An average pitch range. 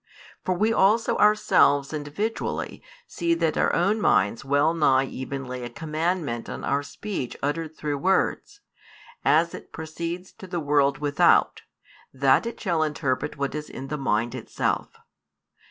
Yes: average, 4.0 semitones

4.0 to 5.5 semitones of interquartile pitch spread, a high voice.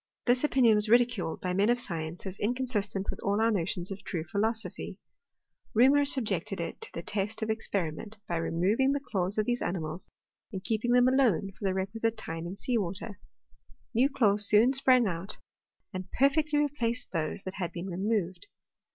Yes: average, 4.6 semitones; high, 210 Hz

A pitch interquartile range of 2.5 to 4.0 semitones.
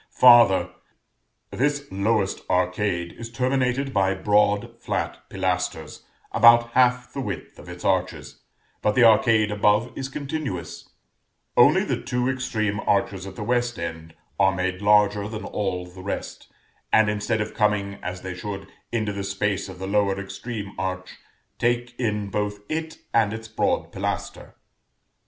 Yes: average, 3.7 semitones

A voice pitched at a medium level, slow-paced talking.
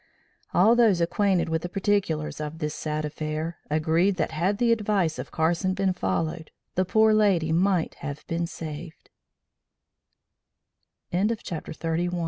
Yes: medium, 170 Hz; slow, 125 wpm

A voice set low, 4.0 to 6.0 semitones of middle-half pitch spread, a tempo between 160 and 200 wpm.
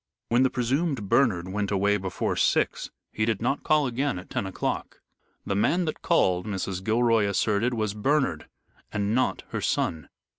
Yes: low, 110 Hz; average, 4.4 semitones; average, 165 wpm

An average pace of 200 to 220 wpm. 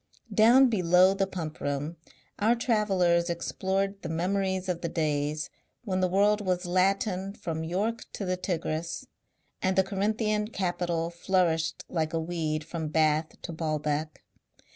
No: average, 140 wpm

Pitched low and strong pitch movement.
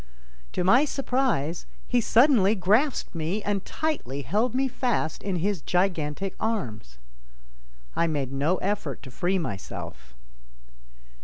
No: high, 190 Hz; wide, 7.3 semitones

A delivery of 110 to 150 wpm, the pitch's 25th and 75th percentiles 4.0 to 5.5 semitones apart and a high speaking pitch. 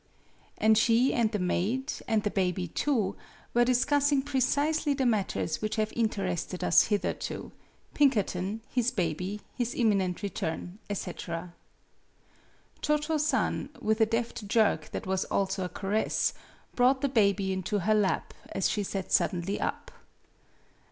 Yes: average, 140 wpm; average, 4.5 semitones; high, 215 Hz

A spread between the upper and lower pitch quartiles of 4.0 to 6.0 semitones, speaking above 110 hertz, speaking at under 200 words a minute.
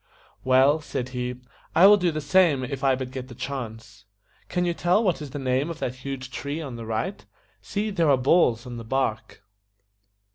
No: average, 4.3 semitones; low, 135 Hz; fast, 205 wpm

